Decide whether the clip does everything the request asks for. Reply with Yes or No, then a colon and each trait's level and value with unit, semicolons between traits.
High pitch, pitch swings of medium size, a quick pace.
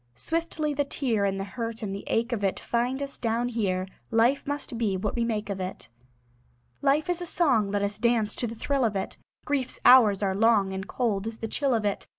Yes: high, 230 Hz; average, 4.4 semitones; fast, 225 wpm